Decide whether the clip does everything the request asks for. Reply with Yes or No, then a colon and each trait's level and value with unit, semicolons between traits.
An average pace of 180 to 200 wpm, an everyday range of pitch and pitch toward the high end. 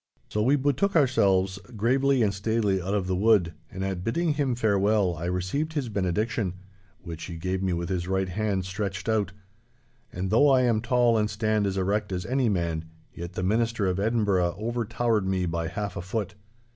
No: average, 190 wpm; average, 3.8 semitones; low, 100 Hz